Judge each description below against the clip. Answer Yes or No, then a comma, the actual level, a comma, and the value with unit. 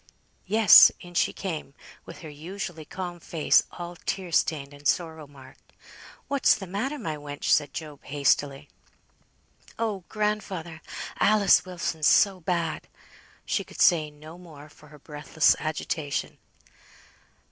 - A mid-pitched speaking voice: Yes, medium, 165 Hz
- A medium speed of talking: No, slow, 130 wpm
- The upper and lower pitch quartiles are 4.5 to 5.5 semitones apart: No, average, 3.9 semitones